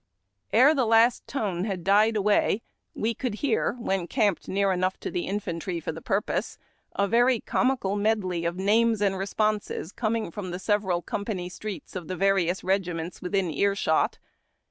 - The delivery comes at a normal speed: Yes, average, 170 wpm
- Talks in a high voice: Yes, high, 200 Hz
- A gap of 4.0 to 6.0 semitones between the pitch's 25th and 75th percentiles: No, average, 3.1 semitones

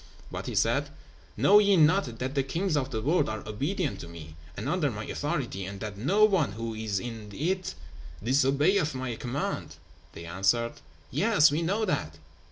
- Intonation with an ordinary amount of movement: No, wide, 8.0 semitones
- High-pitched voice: No, low, 130 Hz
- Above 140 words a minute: Yes, average, 175 wpm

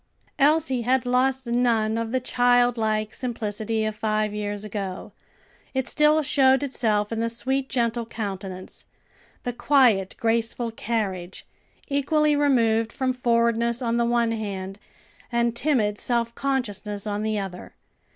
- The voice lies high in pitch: Yes, high, 235 Hz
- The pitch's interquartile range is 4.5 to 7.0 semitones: No, average, 3.1 semitones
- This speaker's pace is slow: Yes, slow, 130 wpm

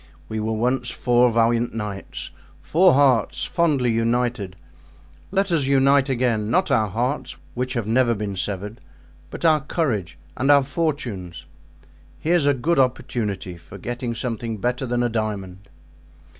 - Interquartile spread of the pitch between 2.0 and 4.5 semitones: Yes, average, 4.0 semitones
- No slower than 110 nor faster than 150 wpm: Yes, average, 140 wpm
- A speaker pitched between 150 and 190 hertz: No, low, 120 Hz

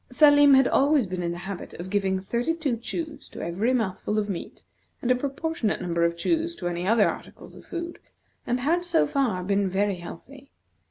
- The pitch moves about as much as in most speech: No, wide, 7.4 semitones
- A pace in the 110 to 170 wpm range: No, average, 195 wpm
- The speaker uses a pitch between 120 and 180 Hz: No, high, 235 Hz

